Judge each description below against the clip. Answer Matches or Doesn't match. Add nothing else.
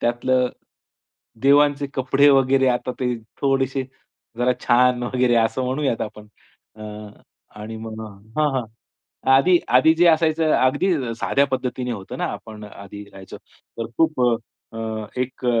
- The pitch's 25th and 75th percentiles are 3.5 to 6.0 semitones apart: Doesn't match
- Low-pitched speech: Matches